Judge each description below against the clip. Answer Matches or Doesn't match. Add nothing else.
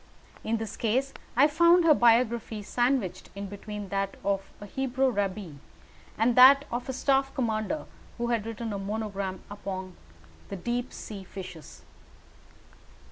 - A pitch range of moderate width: Matches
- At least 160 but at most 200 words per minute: Doesn't match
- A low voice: Doesn't match